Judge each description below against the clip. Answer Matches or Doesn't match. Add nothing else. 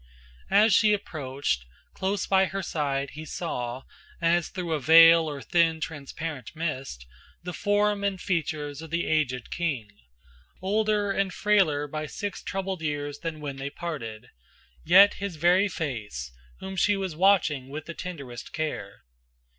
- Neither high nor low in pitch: Matches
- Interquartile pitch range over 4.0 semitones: Matches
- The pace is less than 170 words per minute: Matches